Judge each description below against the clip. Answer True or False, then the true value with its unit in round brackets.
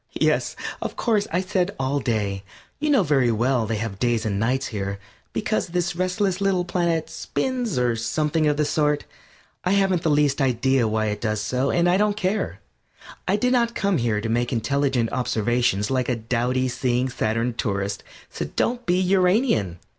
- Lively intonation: True (7.9 semitones)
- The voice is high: False (135 Hz)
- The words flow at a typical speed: True (180 wpm)